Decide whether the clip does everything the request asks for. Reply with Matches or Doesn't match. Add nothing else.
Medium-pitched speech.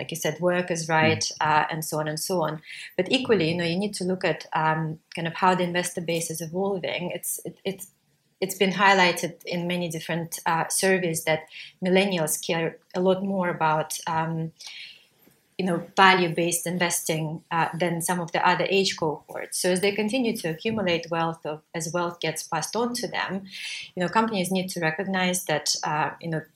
Matches